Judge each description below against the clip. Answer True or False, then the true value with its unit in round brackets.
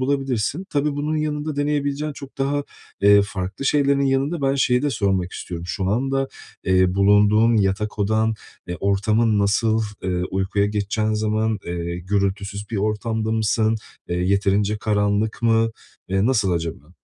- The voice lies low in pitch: True (105 Hz)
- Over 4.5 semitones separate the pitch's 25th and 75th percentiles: True (5.3 semitones)